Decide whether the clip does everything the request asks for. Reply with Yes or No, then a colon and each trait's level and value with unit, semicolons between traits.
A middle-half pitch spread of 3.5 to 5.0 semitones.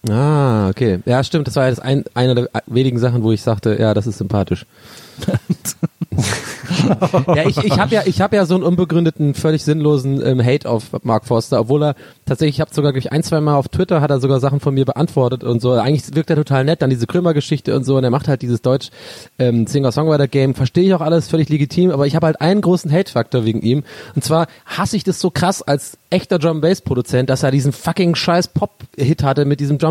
Yes: average, 4.3 semitones